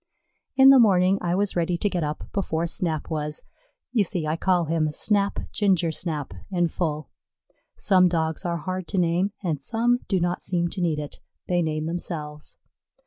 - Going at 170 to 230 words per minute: Yes, average, 180 wpm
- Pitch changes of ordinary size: Yes, average, 3.0 semitones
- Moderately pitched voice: Yes, medium, 175 Hz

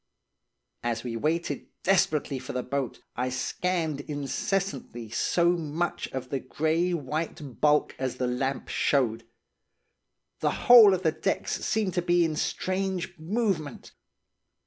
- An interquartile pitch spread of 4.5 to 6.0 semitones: Yes, average, 5.1 semitones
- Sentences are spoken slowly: Yes, slow, 130 wpm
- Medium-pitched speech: Yes, medium, 155 Hz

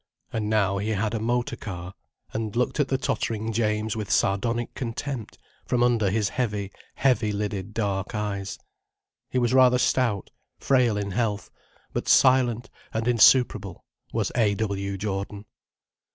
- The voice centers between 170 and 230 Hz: No, low, 110 Hz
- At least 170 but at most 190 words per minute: No, average, 145 wpm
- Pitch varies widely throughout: No, average, 3.0 semitones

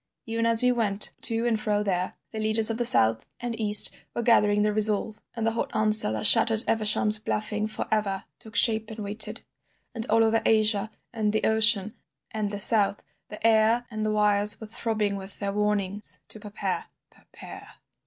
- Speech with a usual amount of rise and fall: No, narrow, 1.3 semitones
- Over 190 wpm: No, average, 185 wpm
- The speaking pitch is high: Yes, high, 215 Hz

